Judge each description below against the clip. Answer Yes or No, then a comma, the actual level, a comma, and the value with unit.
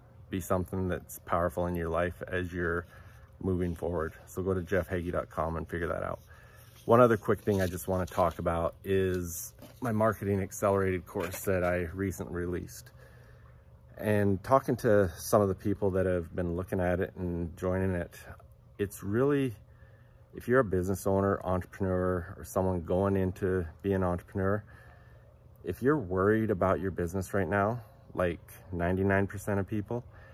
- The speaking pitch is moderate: No, very low, 95 Hz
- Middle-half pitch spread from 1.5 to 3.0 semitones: Yes, narrow, 2.6 semitones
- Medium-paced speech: Yes, average, 160 wpm